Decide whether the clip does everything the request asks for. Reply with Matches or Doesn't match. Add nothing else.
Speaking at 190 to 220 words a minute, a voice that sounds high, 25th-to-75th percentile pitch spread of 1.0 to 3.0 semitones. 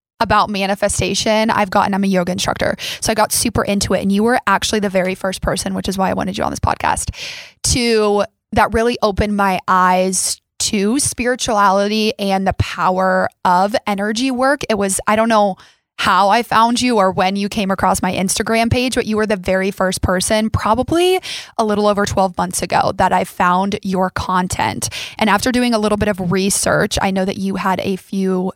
Matches